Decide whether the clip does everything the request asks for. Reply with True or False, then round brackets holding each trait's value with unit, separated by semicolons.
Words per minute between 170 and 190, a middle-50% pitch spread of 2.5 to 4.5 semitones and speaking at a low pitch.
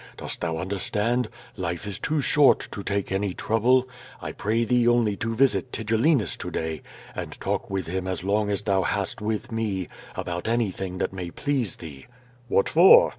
True (175 wpm; 4.2 semitones; 105 Hz)